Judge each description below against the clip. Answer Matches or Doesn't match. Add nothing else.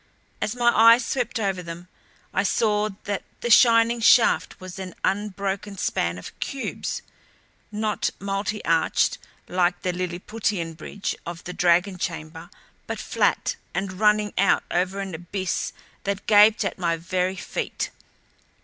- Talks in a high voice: Matches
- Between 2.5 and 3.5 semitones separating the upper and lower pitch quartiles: Matches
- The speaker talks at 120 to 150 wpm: Matches